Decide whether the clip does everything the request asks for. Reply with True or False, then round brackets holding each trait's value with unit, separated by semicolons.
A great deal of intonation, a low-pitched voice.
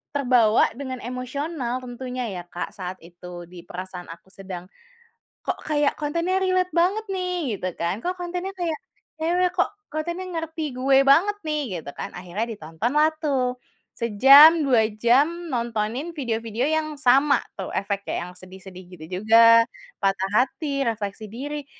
False (7.5 semitones; 255 Hz)